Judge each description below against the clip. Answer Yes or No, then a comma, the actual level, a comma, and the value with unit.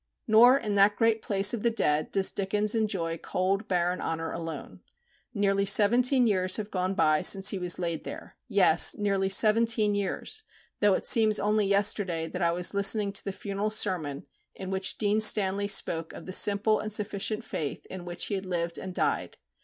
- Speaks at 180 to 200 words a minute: Yes, average, 185 wpm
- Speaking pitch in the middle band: No, high, 200 Hz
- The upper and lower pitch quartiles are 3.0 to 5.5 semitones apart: No, narrow, 2.5 semitones